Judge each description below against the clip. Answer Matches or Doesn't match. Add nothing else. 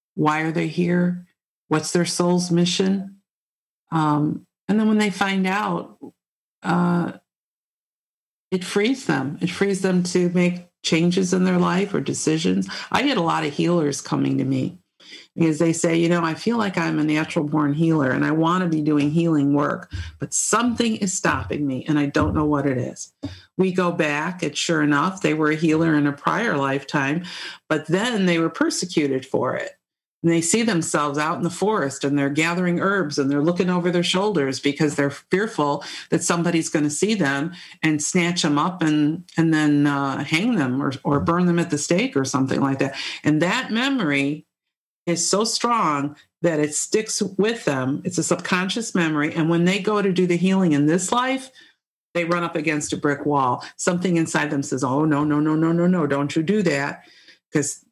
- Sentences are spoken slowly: Doesn't match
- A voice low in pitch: Doesn't match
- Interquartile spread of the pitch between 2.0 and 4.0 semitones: Matches